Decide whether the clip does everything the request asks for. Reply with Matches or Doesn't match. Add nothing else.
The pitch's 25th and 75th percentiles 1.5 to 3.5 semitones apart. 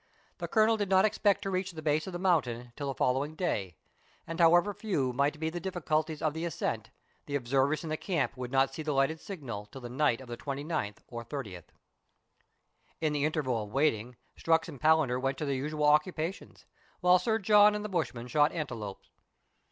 Doesn't match